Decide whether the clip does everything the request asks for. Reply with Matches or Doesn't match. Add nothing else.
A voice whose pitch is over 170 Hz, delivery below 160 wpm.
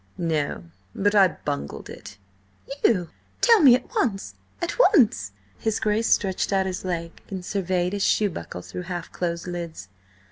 Matches